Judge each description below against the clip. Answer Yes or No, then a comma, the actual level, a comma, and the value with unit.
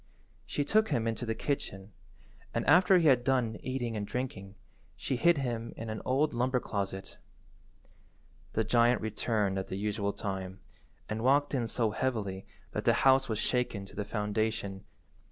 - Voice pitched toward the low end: Yes, low, 115 Hz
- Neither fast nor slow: Yes, average, 165 wpm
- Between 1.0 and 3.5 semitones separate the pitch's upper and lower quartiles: No, average, 4.2 semitones